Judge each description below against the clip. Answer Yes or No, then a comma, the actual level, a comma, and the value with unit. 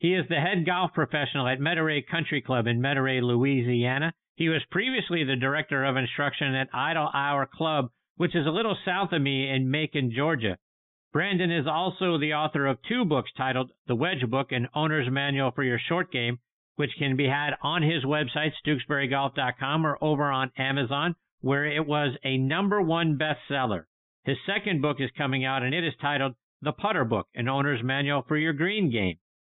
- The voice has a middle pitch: Yes, medium, 145 Hz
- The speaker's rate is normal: Yes, average, 185 wpm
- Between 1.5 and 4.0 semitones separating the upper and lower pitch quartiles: Yes, average, 3.1 semitones